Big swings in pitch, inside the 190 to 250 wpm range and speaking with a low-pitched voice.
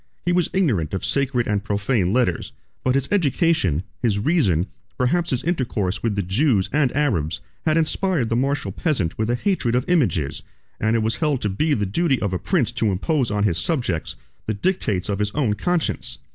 Yes: wide, 7.1 semitones; average, 195 wpm; low, 120 Hz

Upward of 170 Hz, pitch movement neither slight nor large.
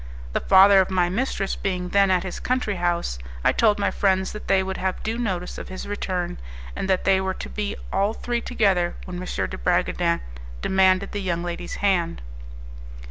No: high, 190 Hz; narrow, 1.9 semitones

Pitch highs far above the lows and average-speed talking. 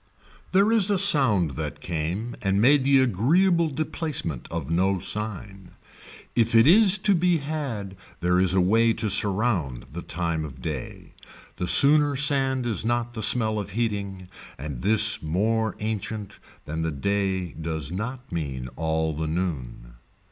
Yes: wide, 7.4 semitones; average, 155 wpm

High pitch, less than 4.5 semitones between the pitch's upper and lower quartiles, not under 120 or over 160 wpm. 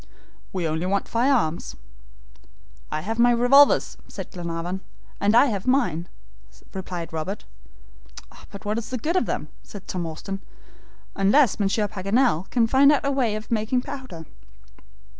No: high, 210 Hz; wide, 5.4 semitones; average, 145 wpm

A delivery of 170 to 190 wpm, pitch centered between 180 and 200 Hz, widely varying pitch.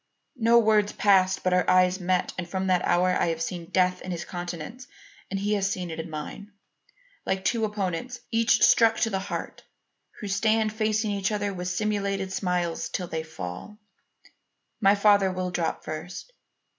No: average, 175 wpm; high, 190 Hz; average, 2.8 semitones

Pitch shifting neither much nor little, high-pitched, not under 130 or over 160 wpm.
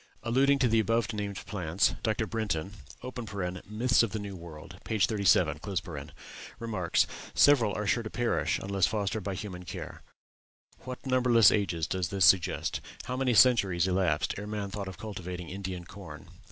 No: average, 3.8 semitones; low, 100 Hz; average, 155 wpm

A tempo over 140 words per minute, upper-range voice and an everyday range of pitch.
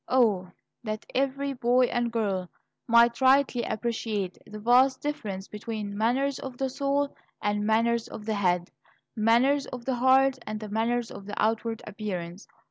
Yes: average, 150 wpm; high, 230 Hz; average, 3.6 semitones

